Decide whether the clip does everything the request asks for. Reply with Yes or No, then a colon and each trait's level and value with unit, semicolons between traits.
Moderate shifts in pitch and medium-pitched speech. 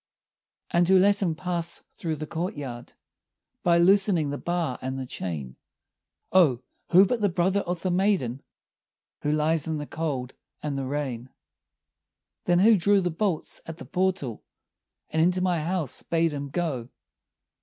Yes: average, 4.4 semitones; medium, 165 Hz